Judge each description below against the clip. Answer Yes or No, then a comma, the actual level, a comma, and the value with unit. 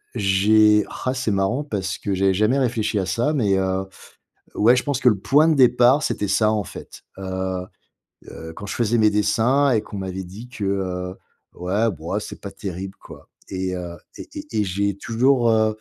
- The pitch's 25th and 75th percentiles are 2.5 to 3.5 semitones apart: No, average, 3.9 semitones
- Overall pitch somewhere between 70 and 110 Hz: Yes, low, 105 Hz